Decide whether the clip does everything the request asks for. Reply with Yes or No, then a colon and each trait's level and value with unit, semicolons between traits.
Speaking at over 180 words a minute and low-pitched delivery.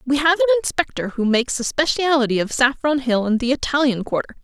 No: fast, 205 wpm; very high, 270 Hz